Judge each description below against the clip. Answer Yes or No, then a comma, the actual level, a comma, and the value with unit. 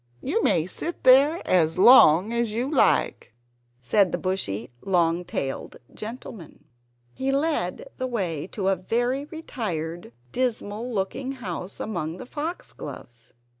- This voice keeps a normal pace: No, slow, 130 wpm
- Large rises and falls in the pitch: Yes, wide, 7.1 semitones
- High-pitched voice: Yes, high, 210 Hz